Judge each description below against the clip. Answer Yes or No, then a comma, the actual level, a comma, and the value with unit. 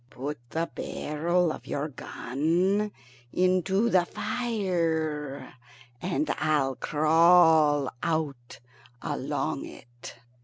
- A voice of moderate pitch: Yes, medium, 160 Hz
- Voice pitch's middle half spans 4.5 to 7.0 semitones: No, average, 3.5 semitones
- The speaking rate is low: Yes, slow, 85 wpm